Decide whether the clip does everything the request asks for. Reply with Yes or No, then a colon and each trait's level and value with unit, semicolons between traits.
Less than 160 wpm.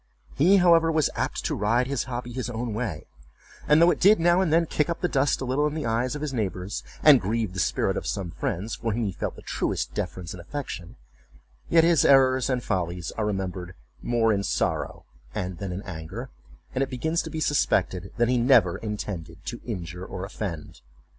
No: fast, 205 wpm